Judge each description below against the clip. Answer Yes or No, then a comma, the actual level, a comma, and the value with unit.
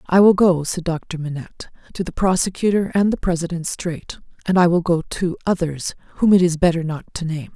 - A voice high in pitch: No, medium, 175 Hz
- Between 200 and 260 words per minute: Yes, fast, 205 wpm